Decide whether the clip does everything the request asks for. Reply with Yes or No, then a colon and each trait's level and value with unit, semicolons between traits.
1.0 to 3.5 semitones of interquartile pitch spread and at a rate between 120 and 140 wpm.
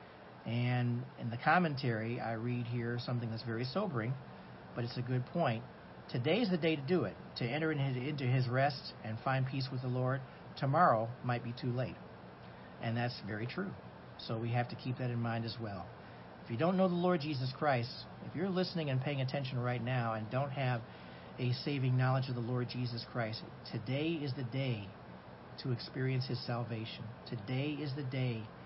No: average, 2.7 semitones; average, 195 wpm